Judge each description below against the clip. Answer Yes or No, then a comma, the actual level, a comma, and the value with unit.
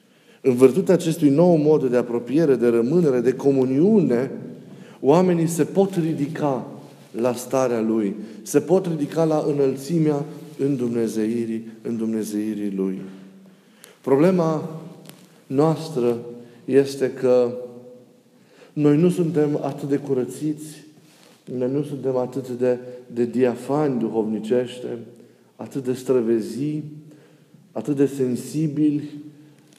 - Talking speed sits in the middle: No, slow, 105 wpm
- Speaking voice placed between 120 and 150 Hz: Yes, medium, 140 Hz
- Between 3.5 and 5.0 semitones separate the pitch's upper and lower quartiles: Yes, average, 3.9 semitones